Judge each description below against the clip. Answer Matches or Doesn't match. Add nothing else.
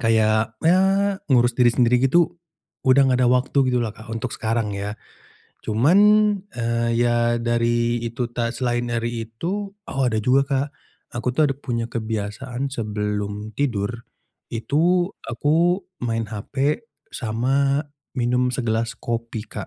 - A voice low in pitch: Matches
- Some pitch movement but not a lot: Matches